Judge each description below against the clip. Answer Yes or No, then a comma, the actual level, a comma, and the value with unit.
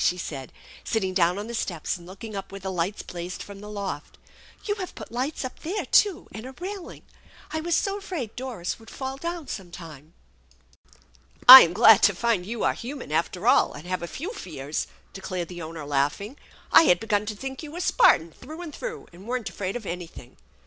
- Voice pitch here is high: Yes, high, 205 Hz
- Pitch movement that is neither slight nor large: No, wide, 7.2 semitones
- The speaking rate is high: Yes, fast, 220 wpm